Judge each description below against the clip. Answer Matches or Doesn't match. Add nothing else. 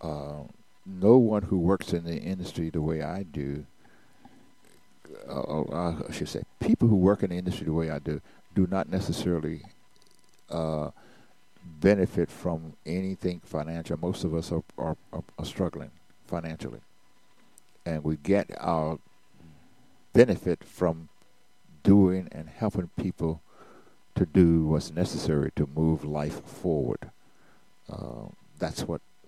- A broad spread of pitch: Doesn't match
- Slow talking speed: Matches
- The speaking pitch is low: Matches